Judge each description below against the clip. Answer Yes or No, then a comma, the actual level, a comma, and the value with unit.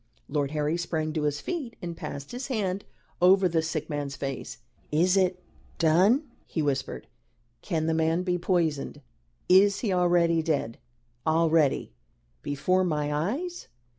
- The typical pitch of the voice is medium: Yes, medium, 165 Hz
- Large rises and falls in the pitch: No, average, 3.5 semitones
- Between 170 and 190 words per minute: No, average, 140 wpm